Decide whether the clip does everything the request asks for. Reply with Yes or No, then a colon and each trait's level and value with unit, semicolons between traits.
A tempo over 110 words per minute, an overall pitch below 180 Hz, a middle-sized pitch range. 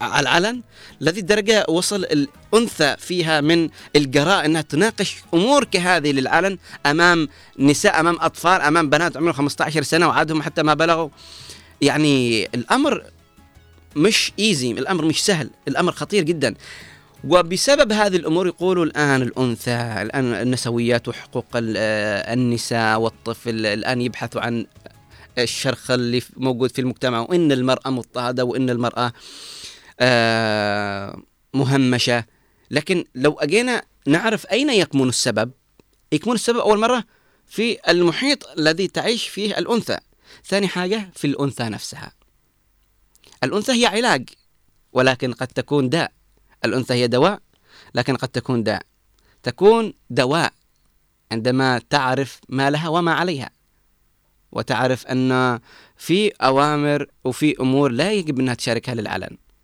No: average, 120 wpm; medium, 140 Hz; wide, 6.1 semitones